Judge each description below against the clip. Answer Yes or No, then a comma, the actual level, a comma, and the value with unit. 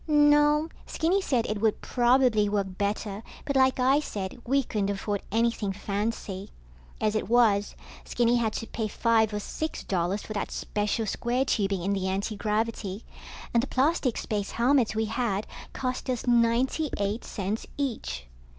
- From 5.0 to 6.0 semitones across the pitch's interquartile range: No, average, 3.8 semitones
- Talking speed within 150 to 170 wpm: Yes, average, 160 wpm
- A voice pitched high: Yes, high, 225 Hz